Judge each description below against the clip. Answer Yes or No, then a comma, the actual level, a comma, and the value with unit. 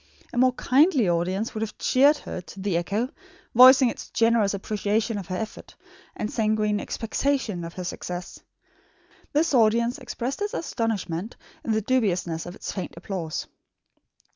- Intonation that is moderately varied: Yes, average, 4.9 semitones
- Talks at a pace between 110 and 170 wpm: Yes, average, 150 wpm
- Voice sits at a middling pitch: No, high, 215 Hz